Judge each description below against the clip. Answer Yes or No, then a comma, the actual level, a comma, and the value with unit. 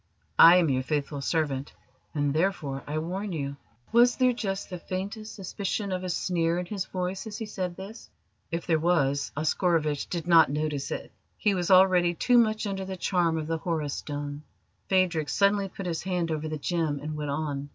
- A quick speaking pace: No, average, 195 wpm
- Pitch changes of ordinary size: Yes, average, 4.0 semitones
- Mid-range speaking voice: Yes, medium, 175 Hz